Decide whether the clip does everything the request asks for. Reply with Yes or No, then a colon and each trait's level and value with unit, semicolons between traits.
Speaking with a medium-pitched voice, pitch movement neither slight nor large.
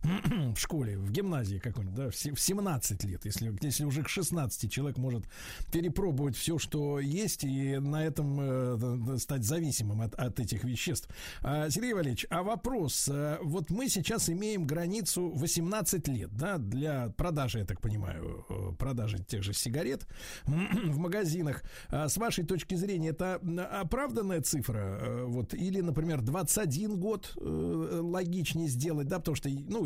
No: medium, 150 Hz; wide, 6.4 semitones